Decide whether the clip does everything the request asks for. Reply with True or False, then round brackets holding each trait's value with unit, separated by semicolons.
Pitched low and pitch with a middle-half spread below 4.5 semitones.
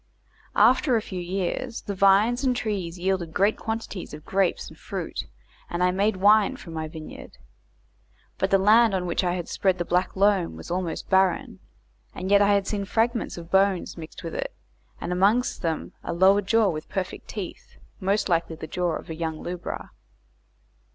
False (190 Hz; 3.0 semitones)